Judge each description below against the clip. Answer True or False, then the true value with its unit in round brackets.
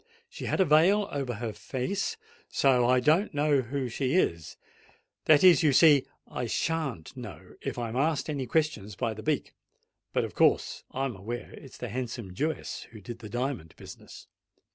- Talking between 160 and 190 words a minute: True (170 wpm)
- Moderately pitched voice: False (130 Hz)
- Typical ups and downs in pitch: True (4.6 semitones)